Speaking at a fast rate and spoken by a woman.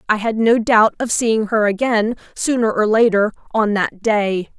No: average, 185 wpm; female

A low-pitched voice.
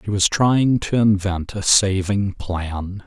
Yes: low, 100 Hz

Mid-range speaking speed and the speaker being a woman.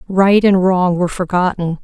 Yes: average, 165 wpm; female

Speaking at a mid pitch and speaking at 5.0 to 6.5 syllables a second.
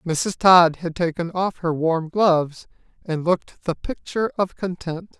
No: medium, 175 Hz; 4.3 syllables/s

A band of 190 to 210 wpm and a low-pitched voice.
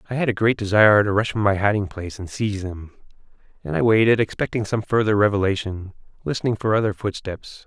Yes: average, 195 wpm; low, 105 Hz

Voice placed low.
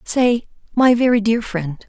No: high, 225 Hz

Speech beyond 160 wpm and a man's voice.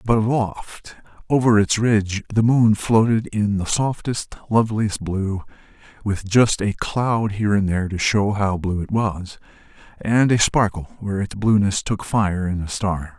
Yes: average, 170 wpm; male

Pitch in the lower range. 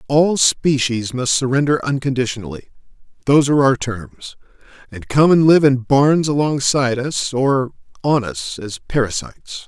Yes: low, 130 Hz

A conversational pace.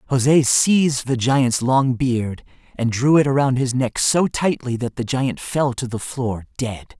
Yes: average, 190 wpm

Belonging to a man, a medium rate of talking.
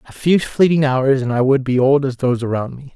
No: male; fast, 265 wpm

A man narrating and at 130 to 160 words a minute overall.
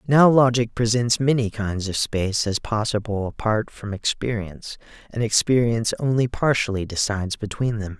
Yes: male; average, 145 wpm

